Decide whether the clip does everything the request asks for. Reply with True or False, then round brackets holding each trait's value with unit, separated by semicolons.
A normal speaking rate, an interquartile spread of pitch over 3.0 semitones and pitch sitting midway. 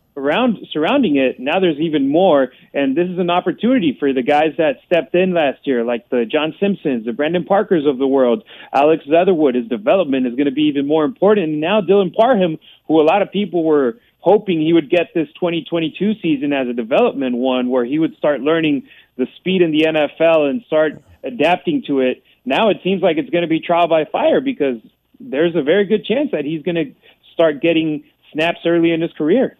False (215 wpm; 3.9 semitones; 160 Hz)